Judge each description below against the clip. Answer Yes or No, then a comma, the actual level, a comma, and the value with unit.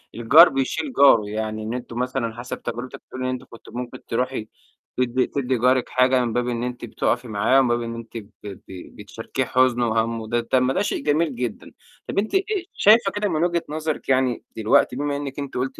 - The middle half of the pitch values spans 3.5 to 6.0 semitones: No, average, 2.7 semitones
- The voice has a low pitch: Yes, low, 125 Hz